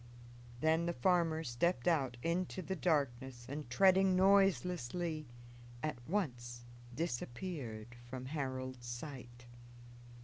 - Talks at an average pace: No, slow, 100 wpm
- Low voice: No, medium, 150 Hz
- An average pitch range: No, wide, 6.4 semitones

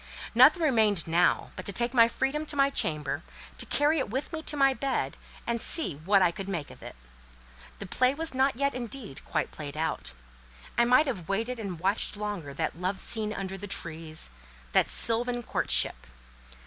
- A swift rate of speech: No, average, 185 wpm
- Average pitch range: No, wide, 6.5 semitones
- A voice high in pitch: Yes, high, 220 Hz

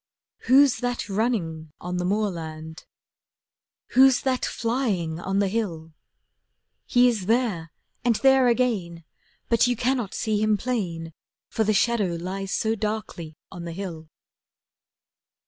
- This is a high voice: Yes, high, 205 Hz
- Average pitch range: No, wide, 5.8 semitones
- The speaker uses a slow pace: Yes, slow, 125 wpm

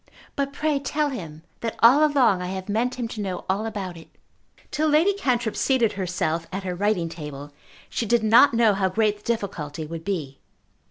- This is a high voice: Yes, high, 210 Hz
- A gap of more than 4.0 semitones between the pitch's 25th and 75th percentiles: Yes, wide, 5.5 semitones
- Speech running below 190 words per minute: No, average, 195 wpm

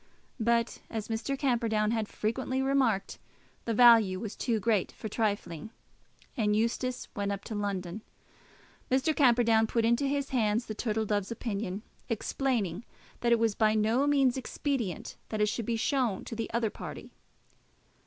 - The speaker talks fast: No, average, 155 wpm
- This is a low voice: No, high, 225 Hz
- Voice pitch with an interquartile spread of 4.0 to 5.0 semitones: No, average, 2.7 semitones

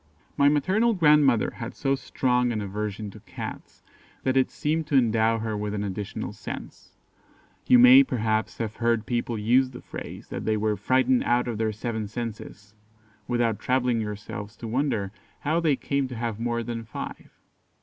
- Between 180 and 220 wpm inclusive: No, average, 170 wpm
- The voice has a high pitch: No, low, 120 Hz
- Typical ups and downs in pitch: Yes, average, 3.5 semitones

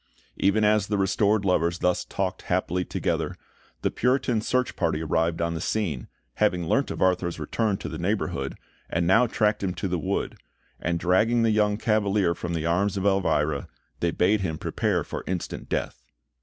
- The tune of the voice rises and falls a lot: No, average, 3.7 semitones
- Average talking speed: Yes, average, 180 wpm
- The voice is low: Yes, very low, 95 Hz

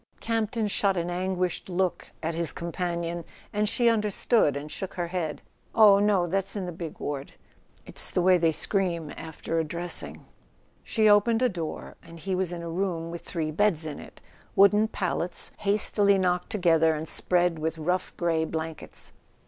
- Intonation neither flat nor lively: Yes, average, 3.3 semitones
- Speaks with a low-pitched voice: No, medium, 180 Hz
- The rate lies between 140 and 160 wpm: No, average, 175 wpm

